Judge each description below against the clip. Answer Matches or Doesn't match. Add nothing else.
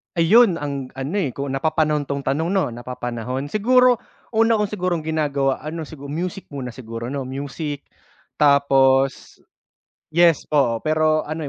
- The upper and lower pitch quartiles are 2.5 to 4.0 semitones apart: Matches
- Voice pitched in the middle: Matches